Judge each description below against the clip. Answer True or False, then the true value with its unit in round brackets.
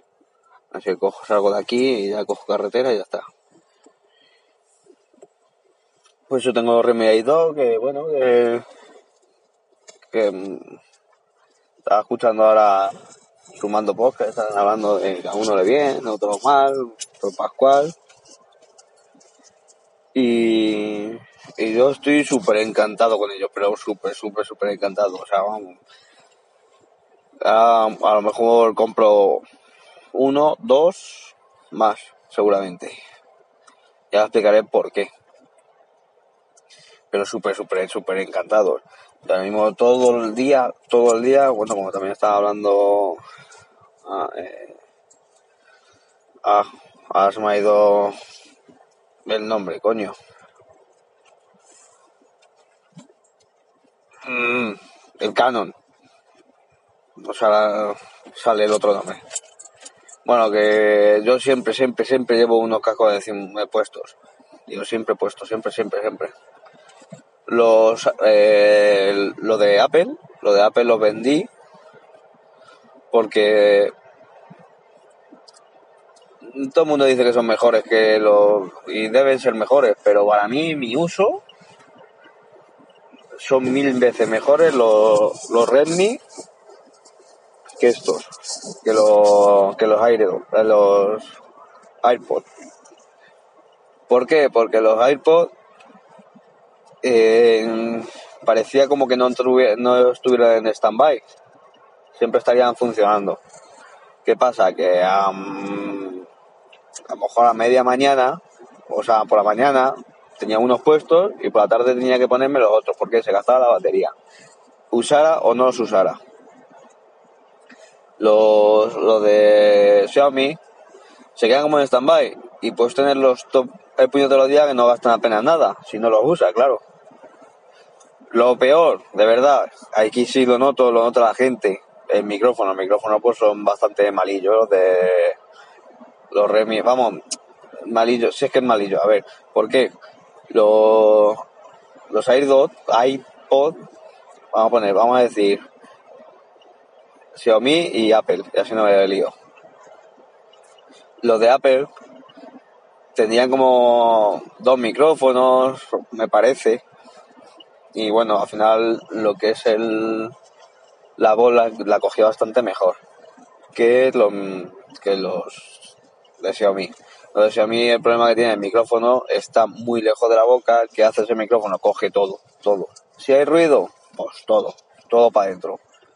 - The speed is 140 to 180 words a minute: False (125 wpm)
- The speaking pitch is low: True (115 Hz)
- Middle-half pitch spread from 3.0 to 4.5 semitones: True (3.9 semitones)